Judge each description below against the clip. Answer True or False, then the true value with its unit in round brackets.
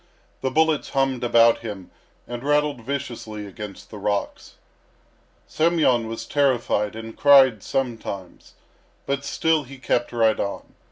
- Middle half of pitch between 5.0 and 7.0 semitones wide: False (3.9 semitones)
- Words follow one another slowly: True (125 wpm)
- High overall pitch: False (120 Hz)